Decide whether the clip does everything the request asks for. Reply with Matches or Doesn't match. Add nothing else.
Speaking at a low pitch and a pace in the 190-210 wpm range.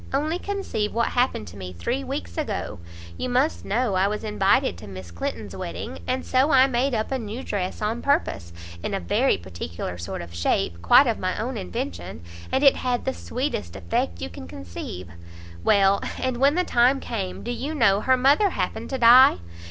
Doesn't match